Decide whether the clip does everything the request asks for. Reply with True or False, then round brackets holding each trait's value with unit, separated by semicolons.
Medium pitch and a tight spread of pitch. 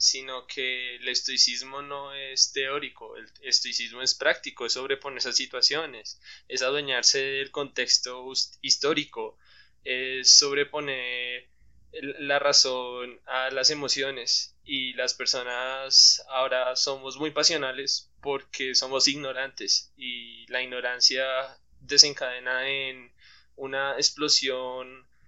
False (130 Hz; 1.8 semitones)